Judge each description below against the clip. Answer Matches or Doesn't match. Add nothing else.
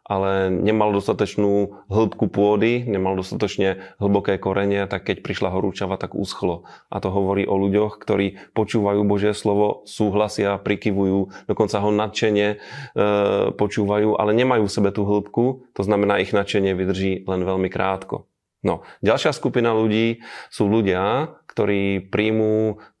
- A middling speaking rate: Matches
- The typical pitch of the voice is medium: Doesn't match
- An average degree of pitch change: Doesn't match